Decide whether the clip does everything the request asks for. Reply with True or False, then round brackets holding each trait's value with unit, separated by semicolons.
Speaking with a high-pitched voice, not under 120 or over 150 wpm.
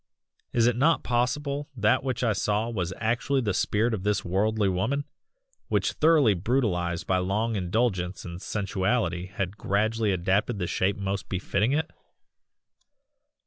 False (105 Hz; 145 wpm)